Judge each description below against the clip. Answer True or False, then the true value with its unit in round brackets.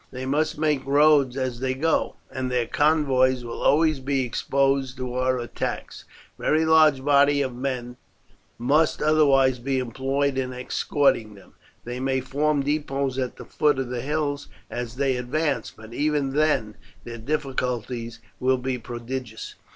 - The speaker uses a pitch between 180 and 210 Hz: False (135 Hz)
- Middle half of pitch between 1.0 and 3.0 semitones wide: True (2.5 semitones)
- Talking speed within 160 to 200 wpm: False (150 wpm)